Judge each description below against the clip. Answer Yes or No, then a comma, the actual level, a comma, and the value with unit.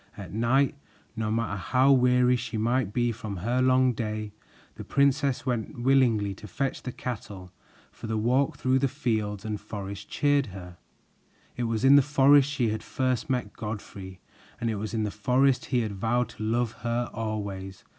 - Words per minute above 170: Yes, average, 180 wpm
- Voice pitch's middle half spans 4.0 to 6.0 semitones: No, average, 3.3 semitones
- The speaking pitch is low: Yes, low, 115 Hz